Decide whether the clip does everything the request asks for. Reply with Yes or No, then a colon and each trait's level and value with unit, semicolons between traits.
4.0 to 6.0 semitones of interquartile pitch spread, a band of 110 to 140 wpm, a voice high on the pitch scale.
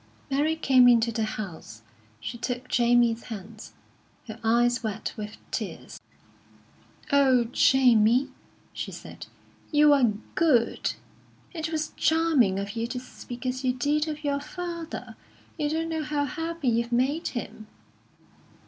Yes: average, 4.5 semitones; slow, 135 wpm; very high, 255 Hz